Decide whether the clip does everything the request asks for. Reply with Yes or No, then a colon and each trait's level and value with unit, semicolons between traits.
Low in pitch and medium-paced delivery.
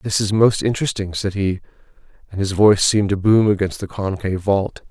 Yes: low, 100 Hz; average, 195 wpm